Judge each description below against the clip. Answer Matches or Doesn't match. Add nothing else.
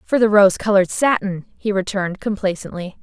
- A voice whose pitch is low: Doesn't match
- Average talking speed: Matches